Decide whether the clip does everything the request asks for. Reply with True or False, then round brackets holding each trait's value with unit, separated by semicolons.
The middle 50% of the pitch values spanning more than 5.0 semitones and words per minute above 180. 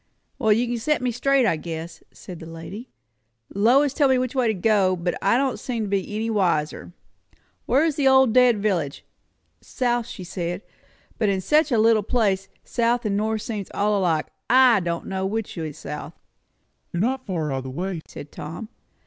True (5.5 semitones; 195 wpm)